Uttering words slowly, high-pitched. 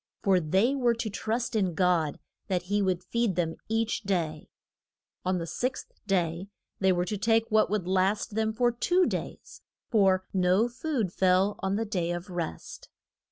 No: average, 170 wpm; high, 195 Hz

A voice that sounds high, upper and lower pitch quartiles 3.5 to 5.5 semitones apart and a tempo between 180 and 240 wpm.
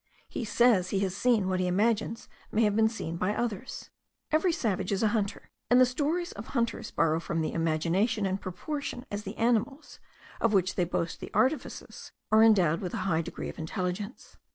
Yes: high, 205 Hz; average, 4.4 semitones; average, 195 wpm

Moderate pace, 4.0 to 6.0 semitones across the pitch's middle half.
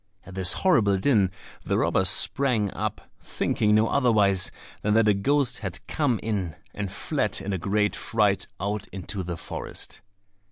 No: average, 160 wpm; average, 2.7 semitones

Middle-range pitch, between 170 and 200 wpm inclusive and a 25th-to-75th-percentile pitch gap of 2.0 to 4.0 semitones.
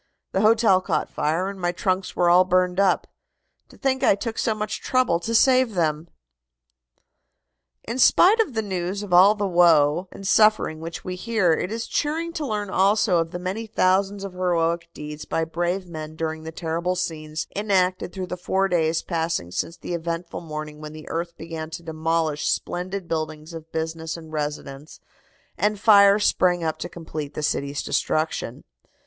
Yes: medium, 175 Hz; average, 180 wpm; average, 3.6 semitones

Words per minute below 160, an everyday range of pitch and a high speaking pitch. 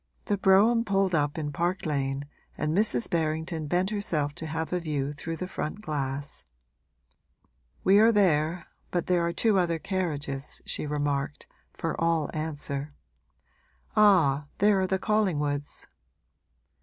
No: average, 140 wpm; average, 4.5 semitones; medium, 160 Hz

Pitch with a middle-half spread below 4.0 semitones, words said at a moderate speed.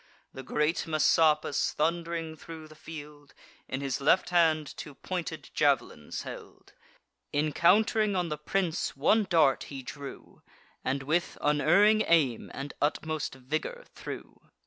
No: average, 2.7 semitones; slow, 125 wpm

